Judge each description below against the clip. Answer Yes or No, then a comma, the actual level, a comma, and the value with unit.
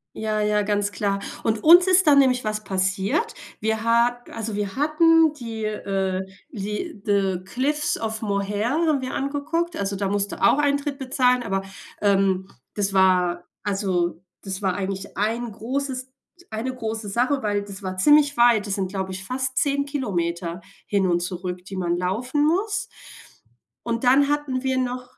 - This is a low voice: No, high, 220 Hz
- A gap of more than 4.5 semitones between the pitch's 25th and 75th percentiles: Yes, wide, 5.5 semitones